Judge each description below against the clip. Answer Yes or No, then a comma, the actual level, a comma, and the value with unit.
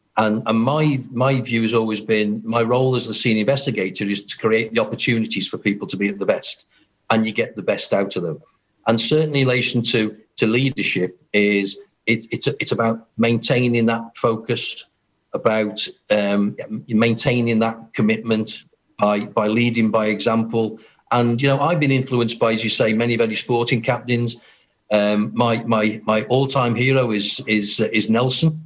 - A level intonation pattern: Yes, narrow, 2.0 semitones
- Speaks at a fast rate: No, average, 175 wpm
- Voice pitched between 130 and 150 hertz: No, low, 115 Hz